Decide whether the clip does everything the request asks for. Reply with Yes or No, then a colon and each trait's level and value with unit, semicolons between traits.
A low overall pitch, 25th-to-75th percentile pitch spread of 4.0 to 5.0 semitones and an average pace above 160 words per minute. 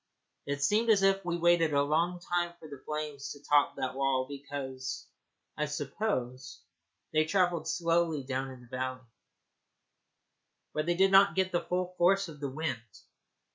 No: medium, 155 Hz; average, 4.3 semitones; average, 170 wpm